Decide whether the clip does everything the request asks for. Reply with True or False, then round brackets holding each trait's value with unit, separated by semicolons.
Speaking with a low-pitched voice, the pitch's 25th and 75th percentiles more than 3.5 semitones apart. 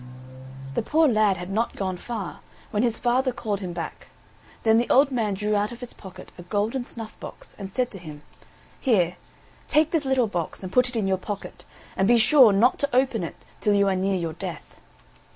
False (215 Hz; 4.4 semitones)